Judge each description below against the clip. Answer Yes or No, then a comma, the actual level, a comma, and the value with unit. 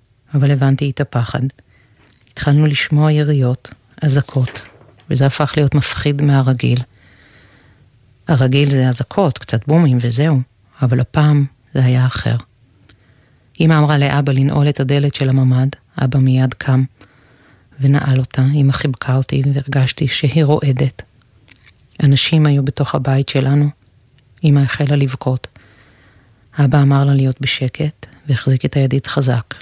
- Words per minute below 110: No, average, 120 wpm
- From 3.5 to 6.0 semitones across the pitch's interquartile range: No, average, 2.8 semitones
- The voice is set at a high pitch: No, low, 135 Hz